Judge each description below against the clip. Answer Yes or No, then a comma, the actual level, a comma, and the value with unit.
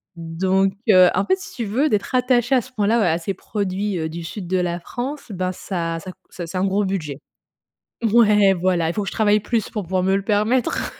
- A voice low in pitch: No, high, 195 Hz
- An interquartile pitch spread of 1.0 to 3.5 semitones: Yes, average, 3.2 semitones